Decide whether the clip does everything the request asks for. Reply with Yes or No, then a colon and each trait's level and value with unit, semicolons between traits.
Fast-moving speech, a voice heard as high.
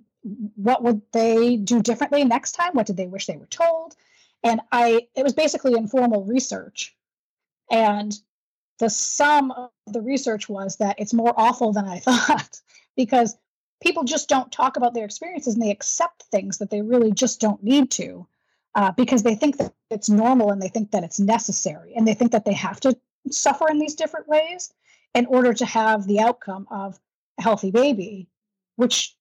No: average, 185 wpm; high, 235 Hz